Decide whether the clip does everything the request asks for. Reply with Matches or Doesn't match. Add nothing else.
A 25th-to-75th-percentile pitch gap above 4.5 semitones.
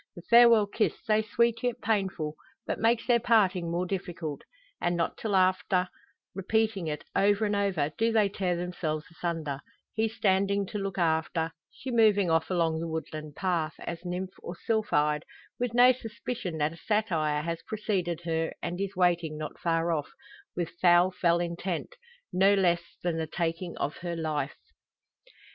Doesn't match